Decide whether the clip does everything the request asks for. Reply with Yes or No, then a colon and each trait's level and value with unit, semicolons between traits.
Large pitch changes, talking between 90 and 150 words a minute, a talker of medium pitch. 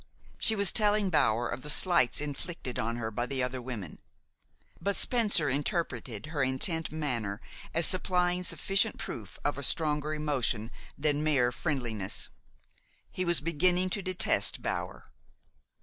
Yes: wide, 6.2 semitones; average, 140 wpm; medium, 150 Hz